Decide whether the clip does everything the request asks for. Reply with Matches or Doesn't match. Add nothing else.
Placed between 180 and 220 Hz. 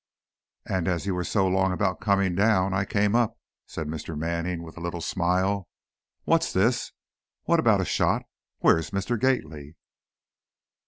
Doesn't match